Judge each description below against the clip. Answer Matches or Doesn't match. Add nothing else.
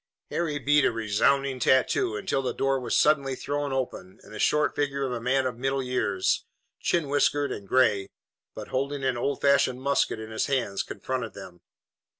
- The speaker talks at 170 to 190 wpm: Matches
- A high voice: Doesn't match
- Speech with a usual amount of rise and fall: Matches